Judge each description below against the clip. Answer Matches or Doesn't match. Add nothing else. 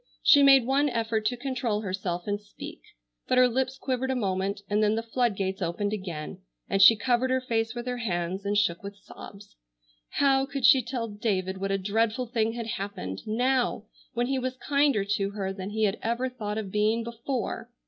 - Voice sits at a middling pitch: Doesn't match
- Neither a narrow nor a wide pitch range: Matches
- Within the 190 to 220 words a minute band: Matches